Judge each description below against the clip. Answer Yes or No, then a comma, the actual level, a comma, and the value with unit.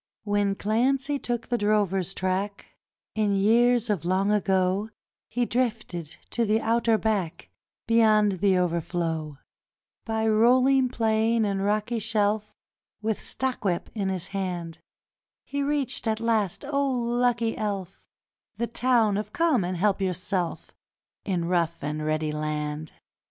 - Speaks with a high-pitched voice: Yes, high, 210 Hz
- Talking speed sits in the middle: No, slow, 130 wpm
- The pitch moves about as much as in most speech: Yes, average, 3.9 semitones